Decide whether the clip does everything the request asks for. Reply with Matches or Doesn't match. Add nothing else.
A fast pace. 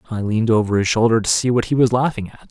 Matches